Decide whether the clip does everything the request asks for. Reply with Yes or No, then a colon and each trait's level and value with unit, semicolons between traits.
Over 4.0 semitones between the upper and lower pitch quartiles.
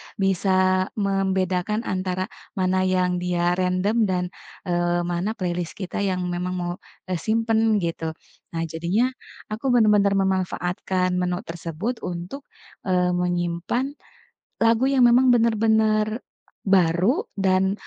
No: average, 3.2 semitones